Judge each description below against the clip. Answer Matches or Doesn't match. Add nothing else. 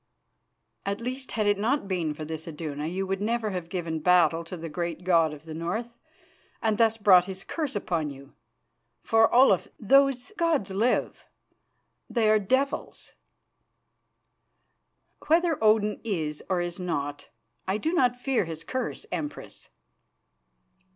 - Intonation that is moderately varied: Doesn't match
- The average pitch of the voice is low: Doesn't match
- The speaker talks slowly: Doesn't match